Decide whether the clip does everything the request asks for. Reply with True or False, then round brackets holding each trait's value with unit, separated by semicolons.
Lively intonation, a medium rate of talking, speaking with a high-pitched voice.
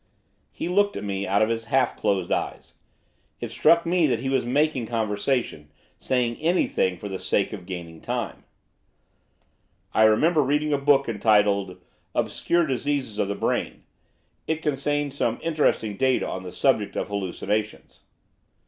False (6.2 semitones; 150 wpm; 120 Hz)